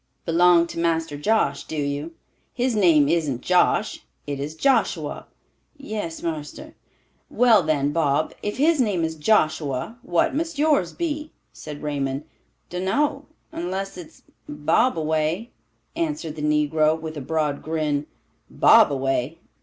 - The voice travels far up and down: Yes, wide, 5.7 semitones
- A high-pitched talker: No, medium, 160 Hz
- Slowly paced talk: Yes, slow, 130 wpm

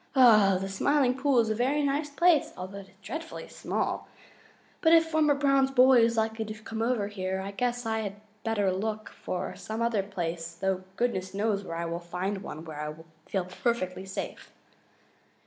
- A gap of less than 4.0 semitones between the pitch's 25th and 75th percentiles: No, average, 4.9 semitones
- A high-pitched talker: Yes, high, 215 Hz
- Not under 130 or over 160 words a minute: No, average, 180 wpm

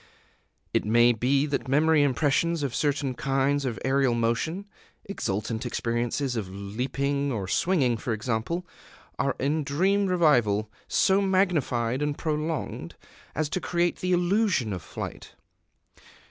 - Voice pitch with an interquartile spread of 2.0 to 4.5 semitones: No, wide, 5.4 semitones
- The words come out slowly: Yes, slow, 130 wpm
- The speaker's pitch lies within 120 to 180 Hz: Yes, medium, 140 Hz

